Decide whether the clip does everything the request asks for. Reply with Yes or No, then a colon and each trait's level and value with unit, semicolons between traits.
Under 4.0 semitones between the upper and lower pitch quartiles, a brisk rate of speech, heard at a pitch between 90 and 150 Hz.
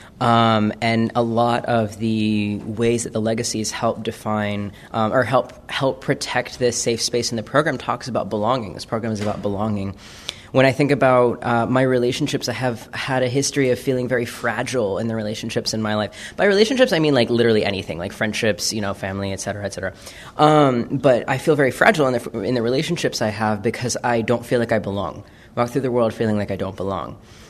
Yes: average, 2.9 semitones; fast, 215 wpm; low, 115 Hz